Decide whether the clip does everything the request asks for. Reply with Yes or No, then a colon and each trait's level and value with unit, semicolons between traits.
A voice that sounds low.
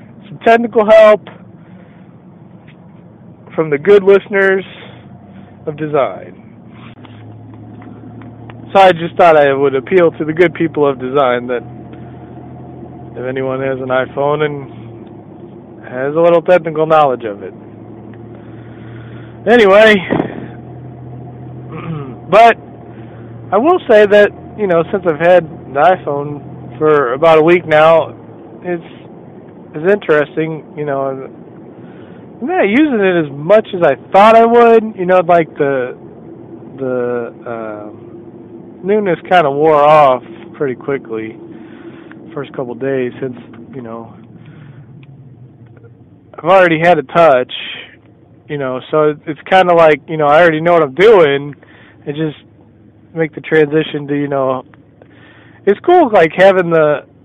No: medium, 150 Hz